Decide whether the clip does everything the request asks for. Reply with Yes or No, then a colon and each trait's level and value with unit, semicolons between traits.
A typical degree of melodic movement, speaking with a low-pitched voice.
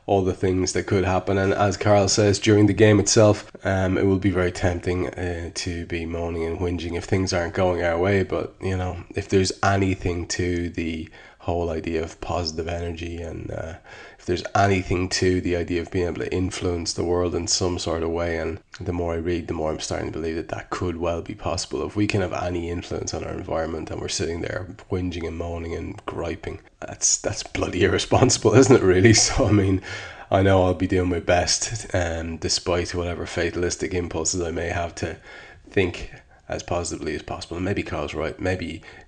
No: narrow, 2.1 semitones; very low, 90 Hz